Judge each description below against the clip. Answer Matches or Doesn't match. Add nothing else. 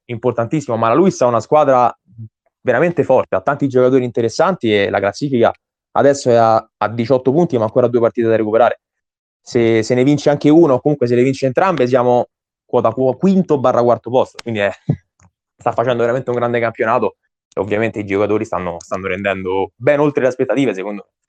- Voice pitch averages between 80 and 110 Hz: Doesn't match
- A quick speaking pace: Matches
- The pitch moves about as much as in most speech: Matches